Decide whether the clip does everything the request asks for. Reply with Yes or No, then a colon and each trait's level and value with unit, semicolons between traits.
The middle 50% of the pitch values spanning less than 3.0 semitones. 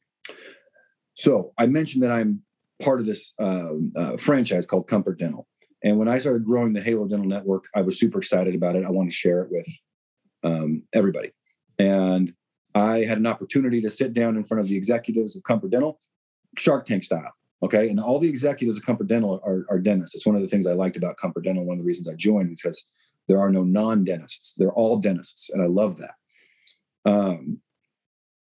No: average, 3.8 semitones